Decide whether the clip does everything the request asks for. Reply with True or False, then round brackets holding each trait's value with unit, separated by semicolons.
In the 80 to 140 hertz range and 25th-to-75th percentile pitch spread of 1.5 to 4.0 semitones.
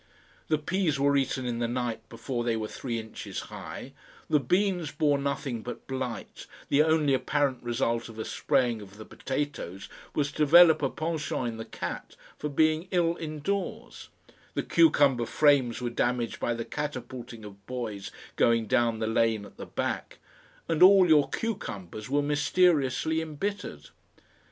False (135 Hz; 4.8 semitones)